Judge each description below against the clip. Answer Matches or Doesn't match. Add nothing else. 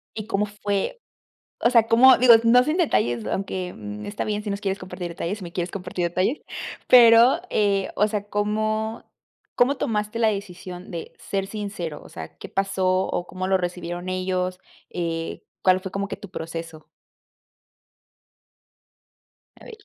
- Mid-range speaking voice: Doesn't match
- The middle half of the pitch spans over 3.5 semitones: Doesn't match